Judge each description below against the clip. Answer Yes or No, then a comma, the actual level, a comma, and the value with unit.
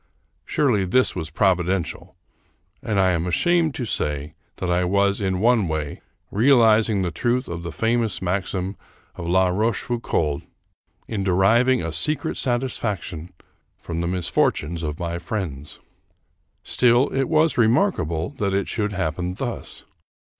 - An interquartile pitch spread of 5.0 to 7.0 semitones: Yes, wide, 5.5 semitones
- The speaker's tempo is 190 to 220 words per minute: No, slow, 135 wpm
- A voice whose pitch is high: No, very low, 95 Hz